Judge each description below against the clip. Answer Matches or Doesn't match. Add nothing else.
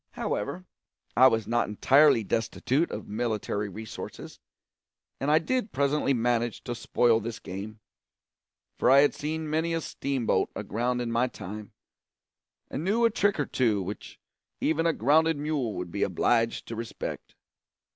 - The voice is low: Matches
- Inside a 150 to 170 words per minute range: Matches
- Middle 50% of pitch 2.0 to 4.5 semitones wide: Doesn't match